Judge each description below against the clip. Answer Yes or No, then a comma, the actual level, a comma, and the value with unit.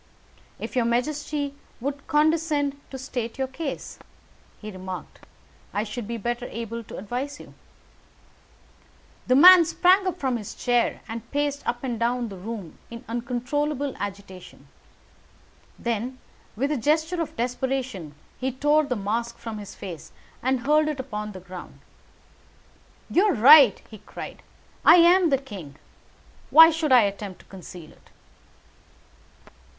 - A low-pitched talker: No, very high, 250 Hz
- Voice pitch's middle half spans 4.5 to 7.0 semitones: Yes, average, 5.1 semitones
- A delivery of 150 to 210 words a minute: No, average, 140 wpm